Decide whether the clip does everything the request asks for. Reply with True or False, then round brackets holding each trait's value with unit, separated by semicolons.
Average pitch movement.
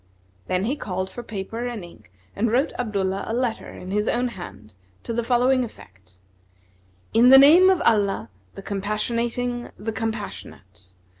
True (4.1 semitones)